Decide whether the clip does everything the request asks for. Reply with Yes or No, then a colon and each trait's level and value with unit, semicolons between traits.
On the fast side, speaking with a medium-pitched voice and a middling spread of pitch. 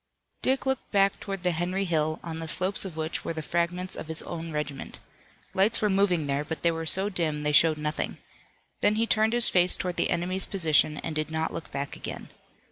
Yes: fast, 215 wpm; medium, 170 Hz; average, 3.4 semitones